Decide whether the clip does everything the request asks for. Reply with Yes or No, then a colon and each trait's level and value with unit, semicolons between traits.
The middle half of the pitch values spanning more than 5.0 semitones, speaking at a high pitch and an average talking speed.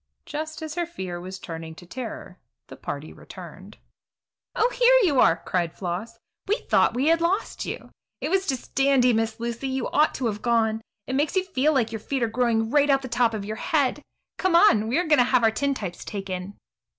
No: wide, 5.6 semitones; very high, 250 Hz; fast, 215 wpm